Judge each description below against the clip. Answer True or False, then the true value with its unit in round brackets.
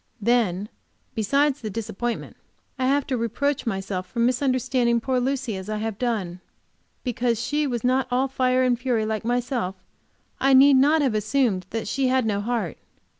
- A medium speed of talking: True (170 wpm)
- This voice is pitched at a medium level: False (245 Hz)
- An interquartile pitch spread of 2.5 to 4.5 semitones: True (3.3 semitones)